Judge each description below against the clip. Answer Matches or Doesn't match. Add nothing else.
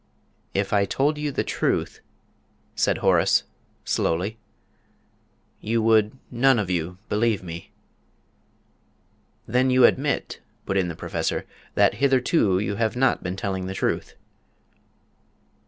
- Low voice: Matches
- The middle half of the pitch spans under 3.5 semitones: Doesn't match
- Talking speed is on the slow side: Matches